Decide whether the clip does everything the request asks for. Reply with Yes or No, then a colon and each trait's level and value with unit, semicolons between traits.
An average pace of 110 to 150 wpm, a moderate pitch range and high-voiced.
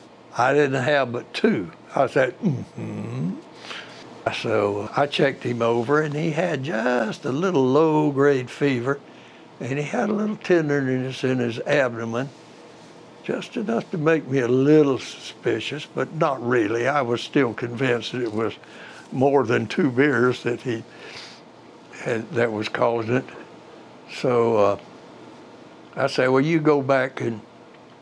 No: average, 145 wpm; average, 3.7 semitones; low, 130 Hz